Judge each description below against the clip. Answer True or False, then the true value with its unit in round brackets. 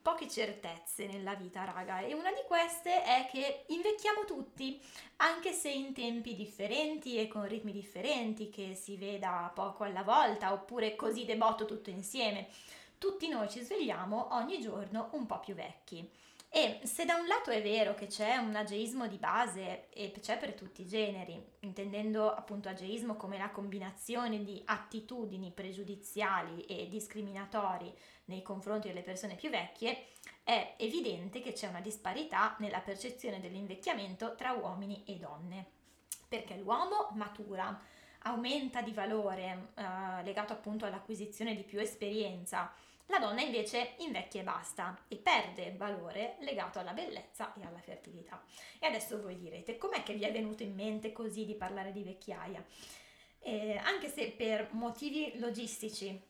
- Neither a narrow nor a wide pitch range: True (3.2 semitones)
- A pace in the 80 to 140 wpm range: False (150 wpm)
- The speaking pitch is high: True (215 Hz)